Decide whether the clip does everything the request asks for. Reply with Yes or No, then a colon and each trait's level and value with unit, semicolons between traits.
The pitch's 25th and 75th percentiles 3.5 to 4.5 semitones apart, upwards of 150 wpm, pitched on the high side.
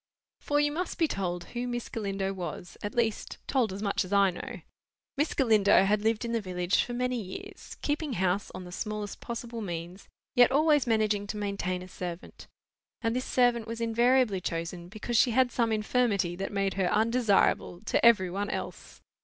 Yes: average, 4.0 semitones; average, 185 wpm; high, 215 Hz